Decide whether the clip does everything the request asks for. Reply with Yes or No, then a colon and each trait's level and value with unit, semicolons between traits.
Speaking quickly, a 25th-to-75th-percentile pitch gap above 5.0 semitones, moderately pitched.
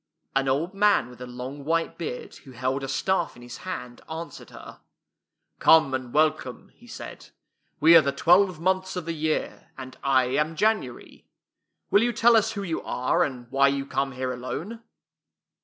No: average, 185 wpm; wide, 5.6 semitones; medium, 150 Hz